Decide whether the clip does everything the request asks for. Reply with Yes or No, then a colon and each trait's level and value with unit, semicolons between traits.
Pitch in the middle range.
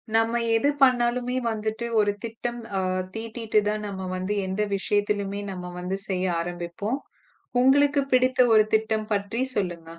No: high, 215 Hz